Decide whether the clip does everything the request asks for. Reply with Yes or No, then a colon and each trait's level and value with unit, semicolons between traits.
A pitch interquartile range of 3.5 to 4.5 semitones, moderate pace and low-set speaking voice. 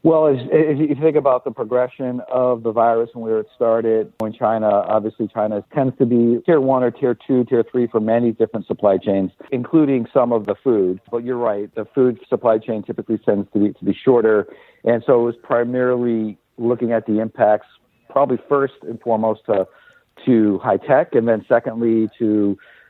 No: narrow, 2.6 semitones; average, 190 wpm; low, 115 Hz